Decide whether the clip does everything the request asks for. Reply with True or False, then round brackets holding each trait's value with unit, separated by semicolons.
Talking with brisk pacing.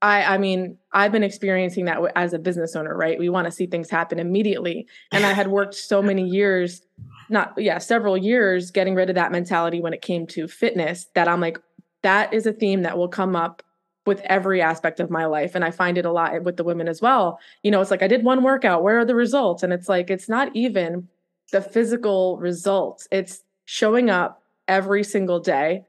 True (220 wpm)